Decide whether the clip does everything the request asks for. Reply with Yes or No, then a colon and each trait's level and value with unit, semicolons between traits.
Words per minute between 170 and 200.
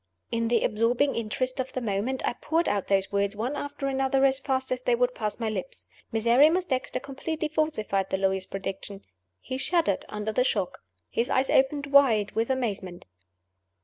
Yes: average, 180 wpm